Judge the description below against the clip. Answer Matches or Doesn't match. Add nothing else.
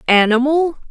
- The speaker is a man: Doesn't match